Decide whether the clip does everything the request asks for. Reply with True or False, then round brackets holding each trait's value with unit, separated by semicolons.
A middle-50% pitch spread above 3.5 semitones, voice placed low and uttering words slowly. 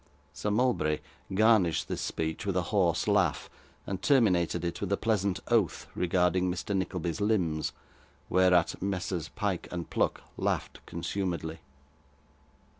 False (2.9 semitones; 90 Hz; 125 wpm)